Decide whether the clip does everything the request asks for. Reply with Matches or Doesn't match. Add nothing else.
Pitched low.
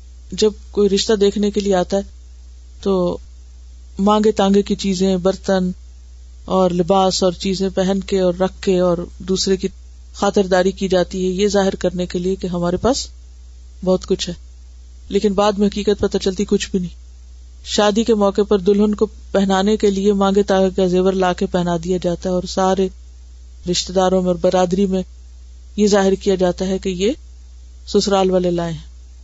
Doesn't match